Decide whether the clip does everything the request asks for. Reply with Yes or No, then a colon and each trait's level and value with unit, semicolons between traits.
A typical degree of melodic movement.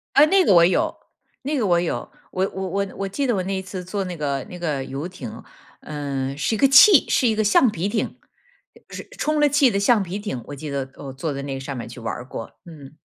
No: wide, 7.4 semitones